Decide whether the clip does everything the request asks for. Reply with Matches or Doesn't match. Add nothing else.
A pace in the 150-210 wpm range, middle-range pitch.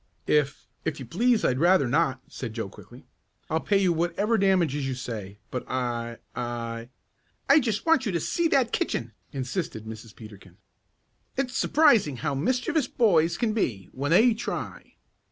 Matches